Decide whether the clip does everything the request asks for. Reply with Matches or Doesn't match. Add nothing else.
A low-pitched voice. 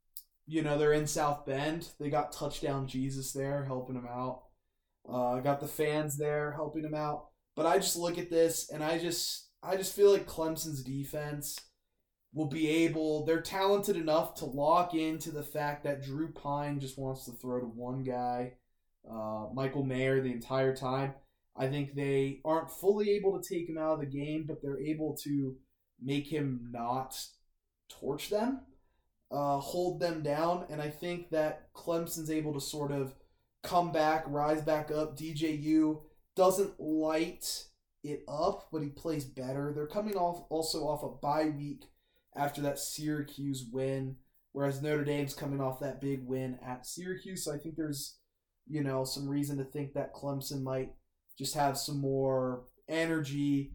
Doesn't match